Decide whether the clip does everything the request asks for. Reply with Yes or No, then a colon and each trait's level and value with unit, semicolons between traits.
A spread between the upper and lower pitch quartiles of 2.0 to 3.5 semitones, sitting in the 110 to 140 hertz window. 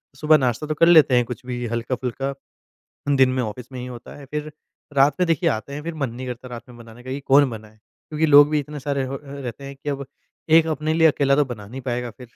Yes: average, 3.2 semitones; low, 135 Hz